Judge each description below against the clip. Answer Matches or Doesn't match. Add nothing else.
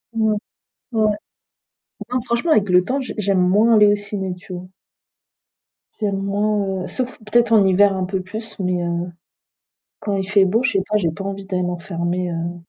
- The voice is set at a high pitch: Matches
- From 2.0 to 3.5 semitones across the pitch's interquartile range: Matches